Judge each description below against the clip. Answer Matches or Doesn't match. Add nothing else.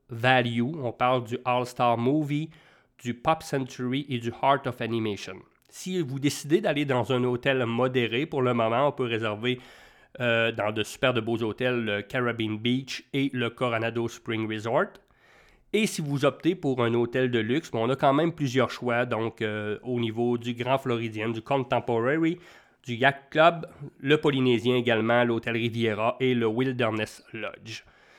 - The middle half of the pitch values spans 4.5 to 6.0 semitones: Doesn't match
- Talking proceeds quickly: Doesn't match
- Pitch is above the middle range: Doesn't match